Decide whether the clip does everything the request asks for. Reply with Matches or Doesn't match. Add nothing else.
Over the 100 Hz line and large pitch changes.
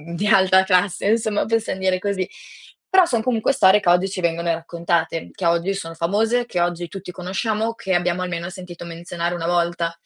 Doesn't match